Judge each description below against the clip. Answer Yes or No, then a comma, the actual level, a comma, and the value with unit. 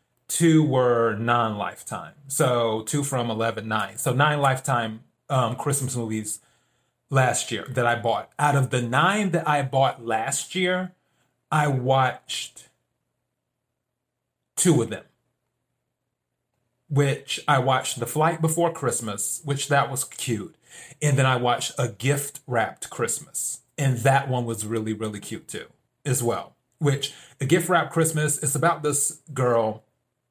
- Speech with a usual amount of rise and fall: Yes, average, 3.6 semitones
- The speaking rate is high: No, average, 145 wpm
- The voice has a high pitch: No, low, 130 Hz